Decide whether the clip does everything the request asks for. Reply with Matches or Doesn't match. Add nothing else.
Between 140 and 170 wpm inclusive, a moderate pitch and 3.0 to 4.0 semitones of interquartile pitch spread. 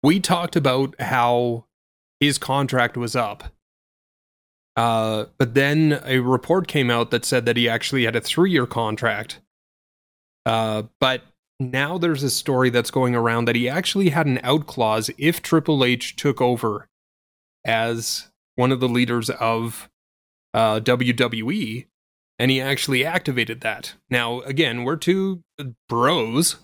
Doesn't match